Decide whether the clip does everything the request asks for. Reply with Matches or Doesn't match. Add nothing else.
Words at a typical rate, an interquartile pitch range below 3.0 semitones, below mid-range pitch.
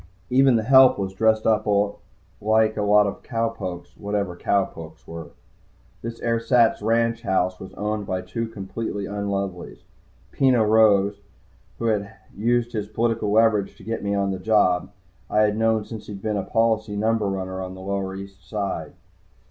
Matches